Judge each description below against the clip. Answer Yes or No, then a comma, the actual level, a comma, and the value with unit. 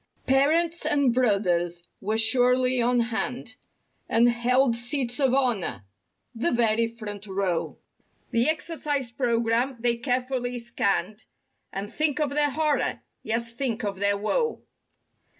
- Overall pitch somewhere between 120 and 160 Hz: No, high, 240 Hz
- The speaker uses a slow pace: Yes, slow, 115 wpm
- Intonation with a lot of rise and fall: No, average, 3.3 semitones